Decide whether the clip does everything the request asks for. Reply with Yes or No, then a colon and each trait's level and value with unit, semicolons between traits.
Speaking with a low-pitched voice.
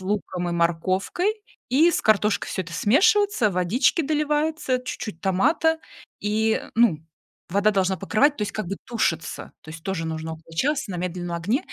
No: high, 205 Hz